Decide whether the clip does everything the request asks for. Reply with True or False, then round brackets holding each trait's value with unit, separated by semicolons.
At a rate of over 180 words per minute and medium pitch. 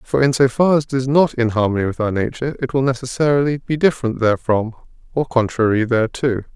False (200 wpm; 125 Hz)